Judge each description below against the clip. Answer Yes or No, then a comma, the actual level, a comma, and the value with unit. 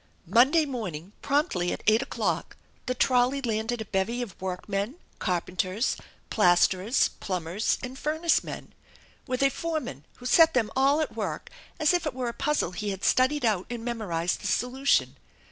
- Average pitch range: No, wide, 6.2 semitones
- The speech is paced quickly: No, average, 160 wpm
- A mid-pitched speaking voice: No, high, 235 Hz